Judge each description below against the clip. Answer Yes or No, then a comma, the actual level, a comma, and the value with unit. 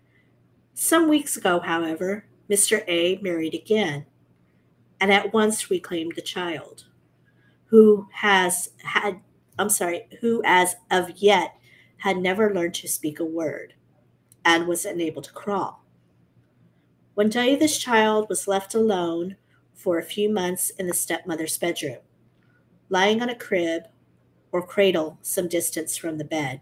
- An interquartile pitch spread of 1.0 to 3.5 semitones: No, average, 3.9 semitones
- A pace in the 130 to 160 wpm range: Yes, average, 140 wpm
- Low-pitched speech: No, medium, 180 Hz